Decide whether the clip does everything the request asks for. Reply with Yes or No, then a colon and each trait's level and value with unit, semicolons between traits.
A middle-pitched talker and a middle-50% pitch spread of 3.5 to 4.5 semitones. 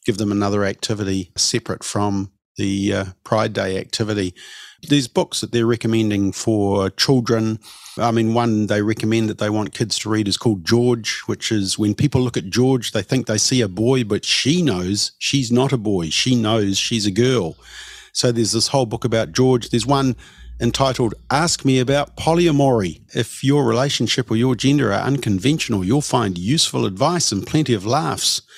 No: low, 115 Hz; average, 3.8 semitones